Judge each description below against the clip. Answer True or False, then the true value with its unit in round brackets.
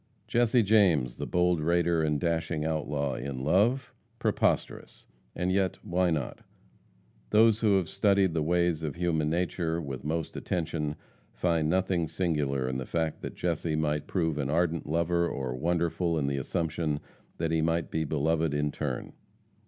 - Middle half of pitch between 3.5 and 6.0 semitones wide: False (2.7 semitones)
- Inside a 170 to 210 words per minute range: False (160 wpm)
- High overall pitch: False (80 Hz)